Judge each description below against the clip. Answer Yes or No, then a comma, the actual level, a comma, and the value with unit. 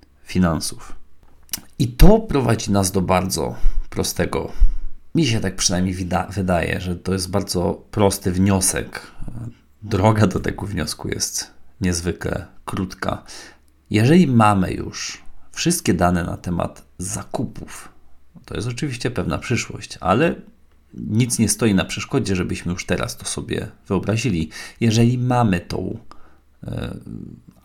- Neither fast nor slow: Yes, average, 120 wpm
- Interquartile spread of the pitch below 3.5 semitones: No, average, 3.9 semitones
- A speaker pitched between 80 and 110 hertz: Yes, very low, 95 Hz